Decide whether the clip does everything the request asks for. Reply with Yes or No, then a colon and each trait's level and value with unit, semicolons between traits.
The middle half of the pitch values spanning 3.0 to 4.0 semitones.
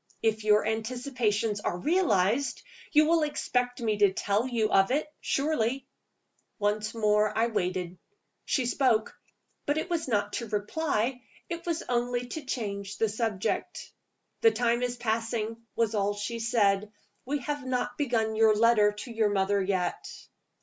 Yes: average, 3.3 semitones